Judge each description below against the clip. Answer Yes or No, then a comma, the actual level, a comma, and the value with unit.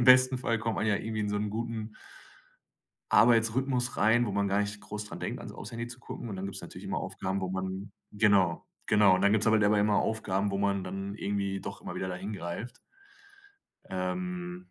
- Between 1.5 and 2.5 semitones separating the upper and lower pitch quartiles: No, average, 2.9 semitones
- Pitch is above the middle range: No, low, 105 Hz